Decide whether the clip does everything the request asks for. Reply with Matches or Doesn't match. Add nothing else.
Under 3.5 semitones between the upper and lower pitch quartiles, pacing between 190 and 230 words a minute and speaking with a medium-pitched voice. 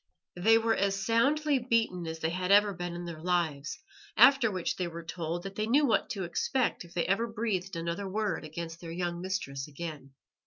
Doesn't match